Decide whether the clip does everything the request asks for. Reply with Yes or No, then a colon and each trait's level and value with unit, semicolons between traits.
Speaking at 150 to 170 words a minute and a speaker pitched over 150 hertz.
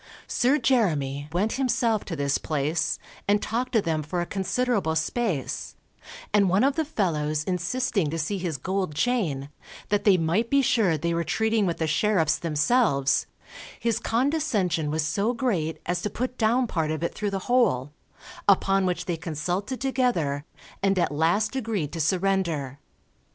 Yes: average, 165 wpm; medium, 185 Hz